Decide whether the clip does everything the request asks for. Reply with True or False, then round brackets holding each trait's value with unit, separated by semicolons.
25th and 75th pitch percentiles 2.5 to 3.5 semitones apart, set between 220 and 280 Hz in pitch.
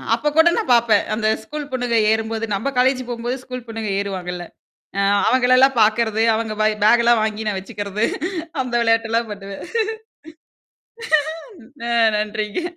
True (2.8 semitones; 225 Hz)